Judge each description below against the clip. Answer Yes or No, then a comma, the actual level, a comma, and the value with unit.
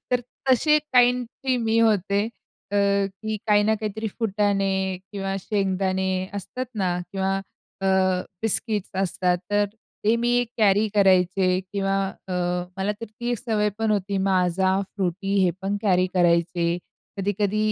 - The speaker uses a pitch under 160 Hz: No, high, 200 Hz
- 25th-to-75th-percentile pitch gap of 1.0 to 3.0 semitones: Yes, narrow, 2.5 semitones